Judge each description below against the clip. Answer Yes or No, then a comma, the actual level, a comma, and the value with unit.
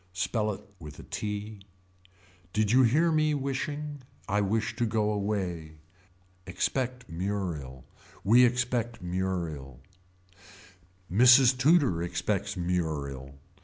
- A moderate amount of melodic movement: No, wide, 6.1 semitones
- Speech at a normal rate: No, slow, 105 wpm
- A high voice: No, low, 105 Hz